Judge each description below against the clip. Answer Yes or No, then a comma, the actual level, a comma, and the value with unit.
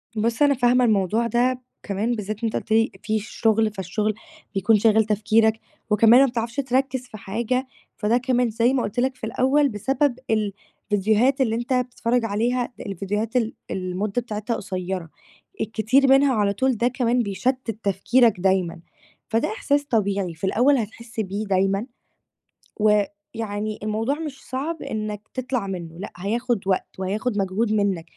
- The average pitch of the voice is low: No, high, 220 Hz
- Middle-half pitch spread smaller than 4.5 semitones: Yes, average, 3.5 semitones